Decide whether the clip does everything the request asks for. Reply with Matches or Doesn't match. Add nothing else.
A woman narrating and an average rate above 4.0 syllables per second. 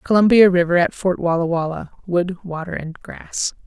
Matches